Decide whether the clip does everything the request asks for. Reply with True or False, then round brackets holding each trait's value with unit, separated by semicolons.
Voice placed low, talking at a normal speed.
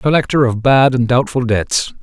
True (125 Hz; 180 wpm)